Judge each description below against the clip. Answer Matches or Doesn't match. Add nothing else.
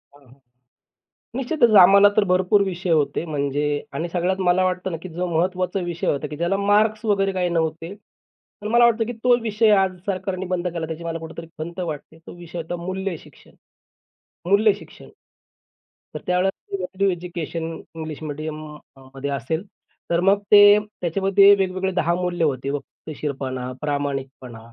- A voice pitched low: Doesn't match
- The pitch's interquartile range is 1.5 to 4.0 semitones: Matches